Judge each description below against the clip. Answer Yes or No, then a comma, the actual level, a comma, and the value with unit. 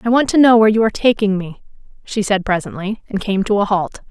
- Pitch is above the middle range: Yes, high, 210 Hz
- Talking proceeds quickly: Yes, fast, 250 wpm